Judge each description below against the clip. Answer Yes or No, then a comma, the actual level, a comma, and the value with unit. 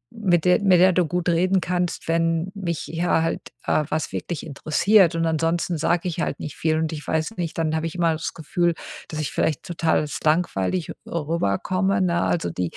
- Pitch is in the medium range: Yes, medium, 165 Hz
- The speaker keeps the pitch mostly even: Yes, narrow, 2.0 semitones